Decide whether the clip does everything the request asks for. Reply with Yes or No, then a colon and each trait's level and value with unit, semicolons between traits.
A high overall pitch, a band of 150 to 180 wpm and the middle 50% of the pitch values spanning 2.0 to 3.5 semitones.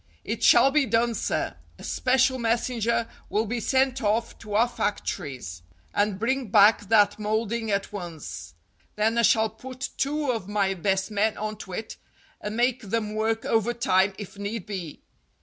Yes: high, 220 Hz; average, 165 wpm; narrow, 2.6 semitones